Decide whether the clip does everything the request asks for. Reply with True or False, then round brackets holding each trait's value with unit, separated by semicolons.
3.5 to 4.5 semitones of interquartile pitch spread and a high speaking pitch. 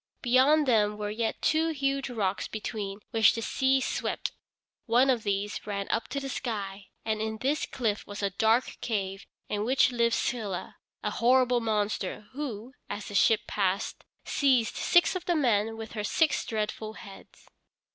True (3.8 semitones; 225 Hz)